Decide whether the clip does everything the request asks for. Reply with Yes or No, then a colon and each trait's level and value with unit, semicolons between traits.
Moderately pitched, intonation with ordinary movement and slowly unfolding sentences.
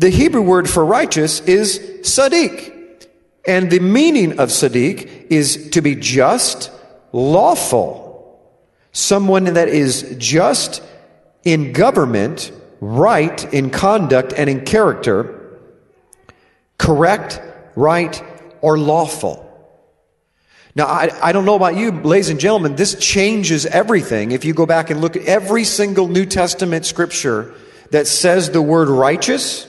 Yes: medium, 175 Hz; average, 4.0 semitones; slow, 125 wpm